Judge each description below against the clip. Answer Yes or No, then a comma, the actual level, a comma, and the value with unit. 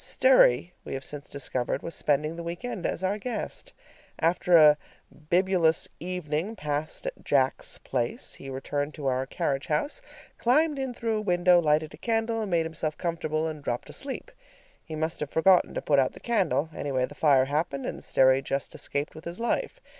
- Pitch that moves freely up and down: No, average, 5.0 semitones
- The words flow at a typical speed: Yes, average, 185 wpm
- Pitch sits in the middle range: Yes, medium, 160 Hz